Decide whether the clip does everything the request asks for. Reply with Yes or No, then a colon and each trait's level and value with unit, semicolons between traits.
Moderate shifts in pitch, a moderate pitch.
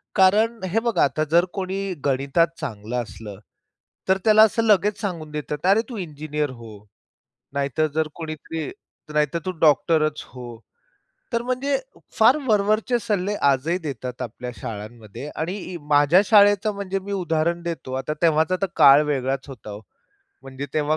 No: wide, 6.2 semitones; medium, 160 Hz